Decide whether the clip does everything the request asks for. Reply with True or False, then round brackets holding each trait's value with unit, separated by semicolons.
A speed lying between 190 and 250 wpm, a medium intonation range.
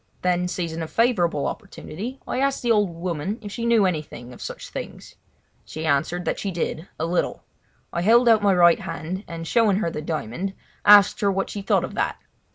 True (200 wpm; 4.0 semitones)